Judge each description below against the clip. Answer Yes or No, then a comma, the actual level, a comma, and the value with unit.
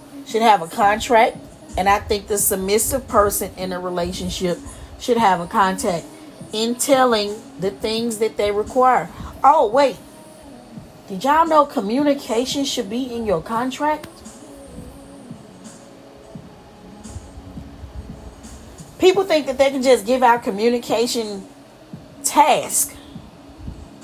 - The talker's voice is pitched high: Yes, high, 230 Hz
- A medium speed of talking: No, slow, 110 wpm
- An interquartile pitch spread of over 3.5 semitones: Yes, average, 4.4 semitones